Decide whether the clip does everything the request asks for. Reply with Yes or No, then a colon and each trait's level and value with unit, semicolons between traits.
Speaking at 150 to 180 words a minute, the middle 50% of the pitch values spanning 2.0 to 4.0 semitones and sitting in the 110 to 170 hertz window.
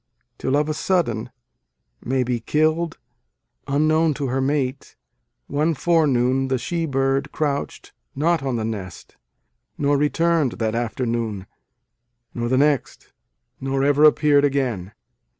No: slow, 135 wpm; average, 3.5 semitones; low, 135 Hz